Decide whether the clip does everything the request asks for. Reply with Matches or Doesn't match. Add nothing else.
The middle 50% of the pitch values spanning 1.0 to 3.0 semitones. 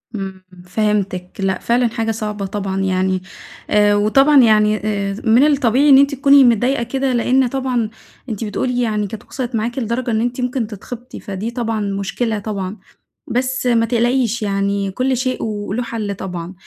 Doesn't match